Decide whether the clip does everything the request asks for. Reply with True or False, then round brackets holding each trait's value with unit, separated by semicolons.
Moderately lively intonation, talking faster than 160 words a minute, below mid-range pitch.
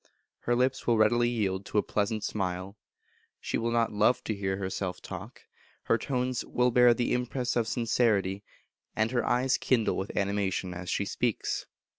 True (3.7 semitones; 170 wpm; 110 Hz)